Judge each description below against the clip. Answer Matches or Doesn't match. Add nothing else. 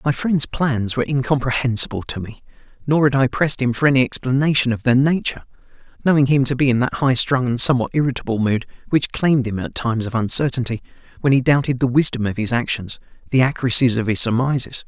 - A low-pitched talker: Matches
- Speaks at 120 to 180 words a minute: Doesn't match